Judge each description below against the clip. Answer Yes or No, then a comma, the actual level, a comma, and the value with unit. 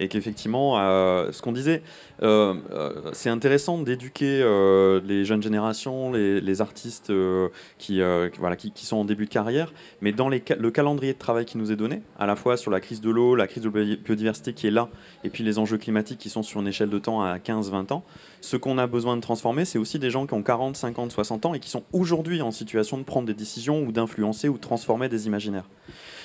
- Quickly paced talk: Yes, fast, 240 wpm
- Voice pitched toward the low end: Yes, low, 115 Hz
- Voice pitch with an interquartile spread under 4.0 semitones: Yes, average, 3.6 semitones